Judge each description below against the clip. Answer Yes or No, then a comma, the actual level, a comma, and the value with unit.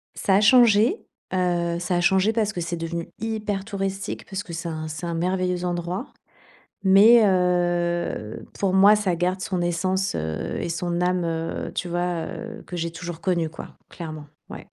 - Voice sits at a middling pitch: Yes, medium, 180 Hz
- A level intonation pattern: Yes, narrow, 2.3 semitones